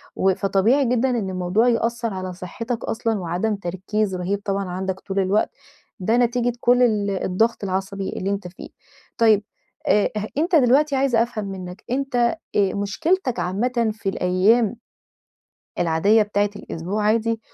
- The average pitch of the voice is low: No, high, 210 Hz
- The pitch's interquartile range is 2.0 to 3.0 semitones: No, average, 3.7 semitones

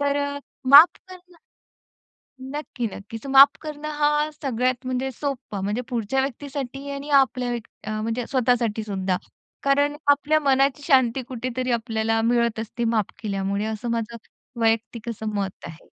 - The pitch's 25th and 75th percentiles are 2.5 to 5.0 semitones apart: Yes, average, 3.8 semitones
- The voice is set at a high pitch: Yes, very high, 250 Hz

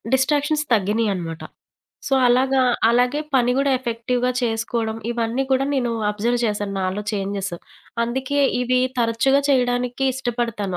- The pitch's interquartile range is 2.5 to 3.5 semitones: Yes, average, 3.0 semitones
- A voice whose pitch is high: Yes, high, 240 Hz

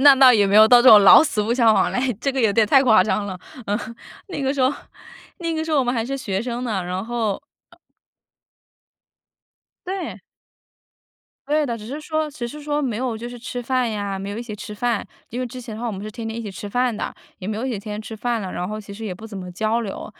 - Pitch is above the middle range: Yes, high, 230 Hz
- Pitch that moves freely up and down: No, average, 3.5 semitones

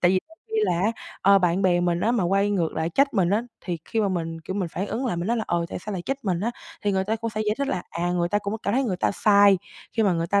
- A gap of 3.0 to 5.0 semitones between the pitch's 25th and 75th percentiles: Yes, average, 3.8 semitones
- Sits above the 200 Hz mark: No, high, 195 Hz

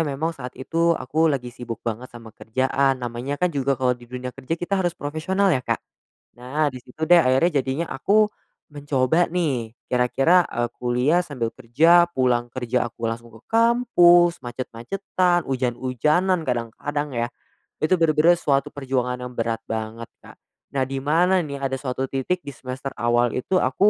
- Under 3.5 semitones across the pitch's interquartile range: No, average, 4.4 semitones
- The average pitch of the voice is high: No, low, 130 Hz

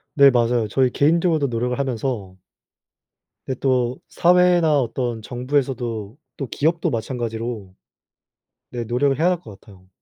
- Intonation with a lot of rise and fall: No, average, 3.7 semitones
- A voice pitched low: Yes, low, 125 Hz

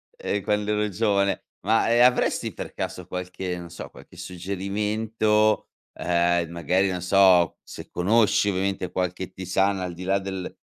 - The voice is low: Yes, very low, 95 Hz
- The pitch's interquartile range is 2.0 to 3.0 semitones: Yes, narrow, 2.4 semitones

